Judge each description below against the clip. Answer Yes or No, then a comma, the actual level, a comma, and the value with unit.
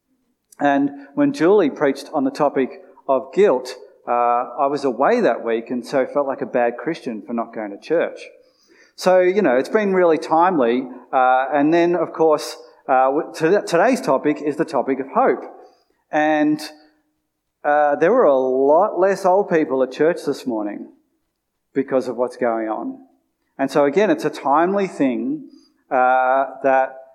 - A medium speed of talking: Yes, average, 165 wpm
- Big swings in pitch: Yes, wide, 6.3 semitones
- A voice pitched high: No, medium, 150 Hz